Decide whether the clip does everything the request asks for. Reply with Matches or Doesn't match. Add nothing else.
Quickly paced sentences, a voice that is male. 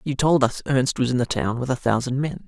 Matches